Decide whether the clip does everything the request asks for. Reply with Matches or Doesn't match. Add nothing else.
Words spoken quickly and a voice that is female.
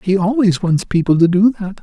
Doesn't match